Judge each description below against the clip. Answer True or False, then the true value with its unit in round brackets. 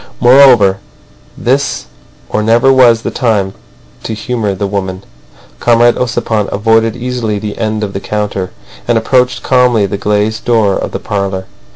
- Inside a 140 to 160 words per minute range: True (150 wpm)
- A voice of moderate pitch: False (110 Hz)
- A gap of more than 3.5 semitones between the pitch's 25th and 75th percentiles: False (3.0 semitones)